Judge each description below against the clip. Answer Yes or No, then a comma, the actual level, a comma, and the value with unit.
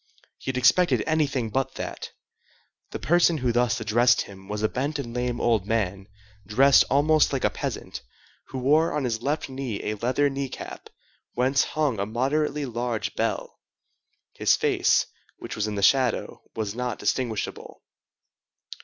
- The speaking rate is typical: Yes, average, 160 wpm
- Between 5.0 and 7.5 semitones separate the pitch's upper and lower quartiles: No, average, 4.0 semitones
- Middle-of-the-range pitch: No, low, 125 Hz